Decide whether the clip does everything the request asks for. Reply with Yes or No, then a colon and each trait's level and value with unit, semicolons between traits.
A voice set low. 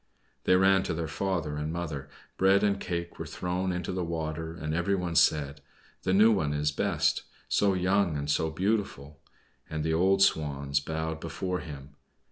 Yes: very low, 80 Hz